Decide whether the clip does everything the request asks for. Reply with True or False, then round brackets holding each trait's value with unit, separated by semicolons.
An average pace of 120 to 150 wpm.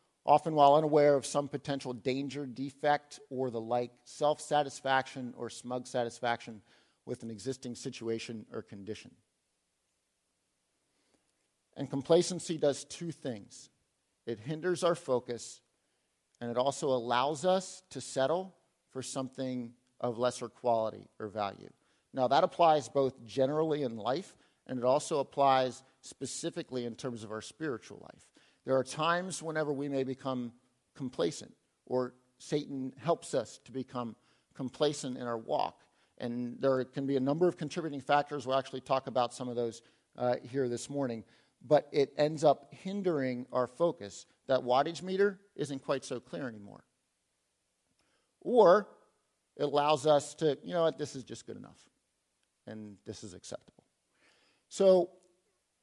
True (145 wpm)